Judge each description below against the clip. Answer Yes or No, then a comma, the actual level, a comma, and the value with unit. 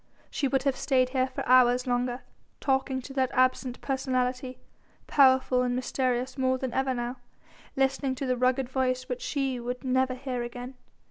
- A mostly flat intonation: Yes, narrow, 1.0 semitones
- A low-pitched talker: No, very high, 255 Hz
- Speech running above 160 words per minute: Yes, average, 170 wpm